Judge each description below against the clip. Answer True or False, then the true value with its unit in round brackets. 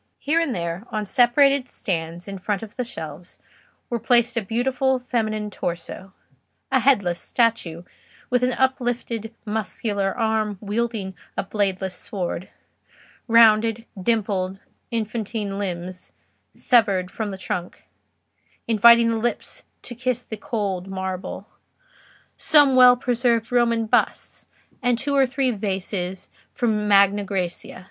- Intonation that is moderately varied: True (3.9 semitones)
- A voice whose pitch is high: True (220 Hz)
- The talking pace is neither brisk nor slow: False (125 wpm)